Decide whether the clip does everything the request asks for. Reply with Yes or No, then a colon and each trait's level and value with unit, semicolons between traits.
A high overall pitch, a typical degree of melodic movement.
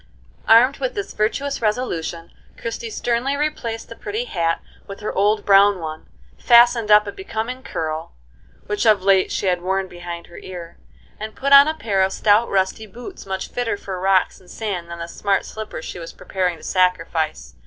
Yes: high, 205 Hz; average, 4.6 semitones